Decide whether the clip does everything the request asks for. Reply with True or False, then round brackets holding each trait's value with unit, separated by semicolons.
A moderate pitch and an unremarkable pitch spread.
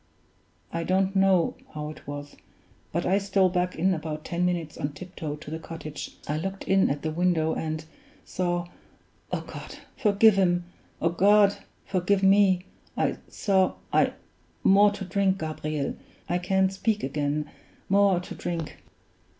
True (180 Hz; 3.5 semitones)